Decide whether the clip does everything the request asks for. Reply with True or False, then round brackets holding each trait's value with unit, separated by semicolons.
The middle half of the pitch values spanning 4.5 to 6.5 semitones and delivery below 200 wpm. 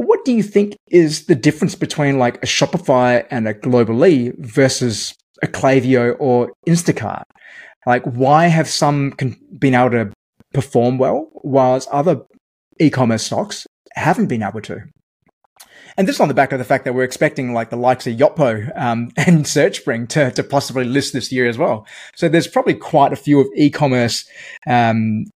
False (3.5 semitones; 175 wpm)